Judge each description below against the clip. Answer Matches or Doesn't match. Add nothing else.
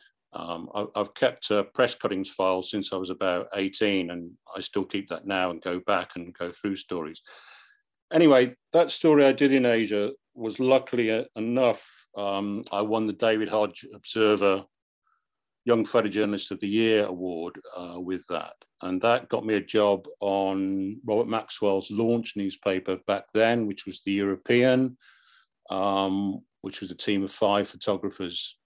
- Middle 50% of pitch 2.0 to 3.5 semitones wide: Matches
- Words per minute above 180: Doesn't match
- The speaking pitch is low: Matches